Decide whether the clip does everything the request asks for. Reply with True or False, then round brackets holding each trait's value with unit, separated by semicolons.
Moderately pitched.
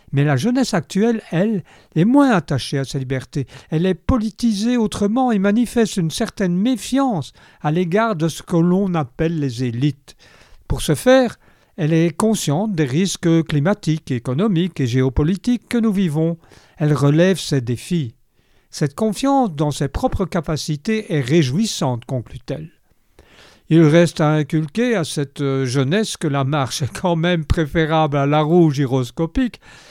True (165 Hz)